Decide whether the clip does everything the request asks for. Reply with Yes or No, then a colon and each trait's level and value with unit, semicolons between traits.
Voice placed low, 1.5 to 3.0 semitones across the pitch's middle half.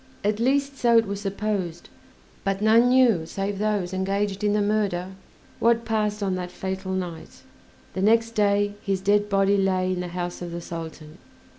No: high, 200 Hz; narrow, 2.5 semitones